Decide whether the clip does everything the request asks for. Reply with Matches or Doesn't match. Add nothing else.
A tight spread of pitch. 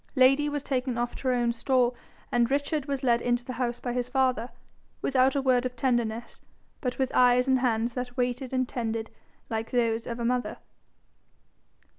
Matches